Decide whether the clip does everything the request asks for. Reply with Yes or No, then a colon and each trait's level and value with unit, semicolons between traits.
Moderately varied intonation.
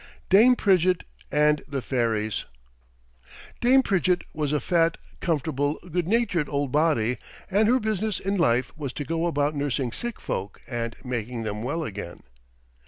No: wide, 6.5 semitones